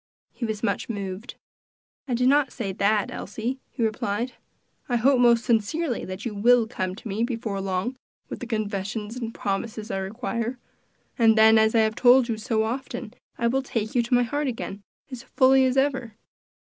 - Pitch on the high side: Yes, high, 230 Hz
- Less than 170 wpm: No, average, 185 wpm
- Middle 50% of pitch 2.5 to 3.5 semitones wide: Yes, average, 2.8 semitones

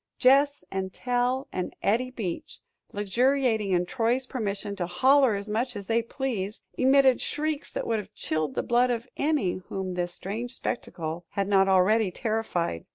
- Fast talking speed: No, average, 160 wpm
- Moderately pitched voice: No, high, 220 Hz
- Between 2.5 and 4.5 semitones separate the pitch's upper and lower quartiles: No, average, 4.9 semitones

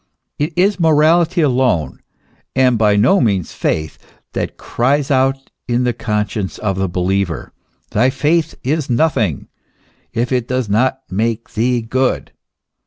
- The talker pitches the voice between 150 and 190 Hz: No, low, 125 Hz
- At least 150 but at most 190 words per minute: No, slow, 135 wpm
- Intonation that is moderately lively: Yes, average, 4.7 semitones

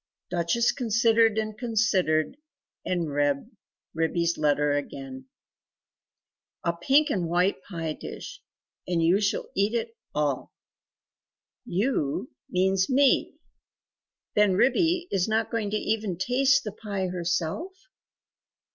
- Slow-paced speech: Yes, slow, 115 wpm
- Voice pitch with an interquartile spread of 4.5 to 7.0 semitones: Yes, average, 5.2 semitones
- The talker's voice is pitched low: No, high, 195 Hz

